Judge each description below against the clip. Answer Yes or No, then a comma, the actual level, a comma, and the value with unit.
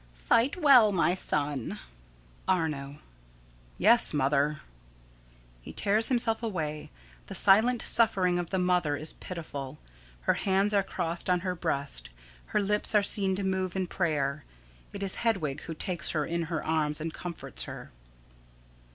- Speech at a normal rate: Yes, average, 150 wpm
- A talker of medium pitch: Yes, medium, 175 Hz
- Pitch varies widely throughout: No, average, 4.8 semitones